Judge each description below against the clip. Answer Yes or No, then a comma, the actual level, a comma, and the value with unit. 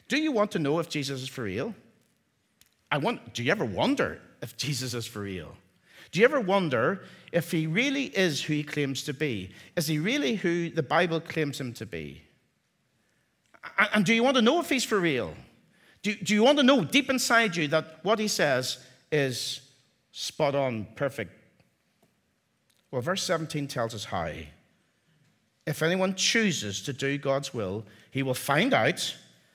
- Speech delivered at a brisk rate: No, average, 180 wpm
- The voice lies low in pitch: No, medium, 150 Hz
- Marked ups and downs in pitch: Yes, wide, 7.2 semitones